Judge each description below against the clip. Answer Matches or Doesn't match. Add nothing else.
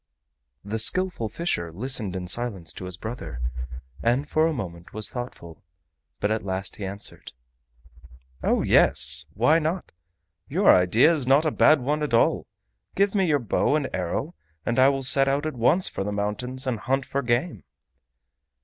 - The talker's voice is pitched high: Doesn't match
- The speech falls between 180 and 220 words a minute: Doesn't match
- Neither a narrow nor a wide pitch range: Doesn't match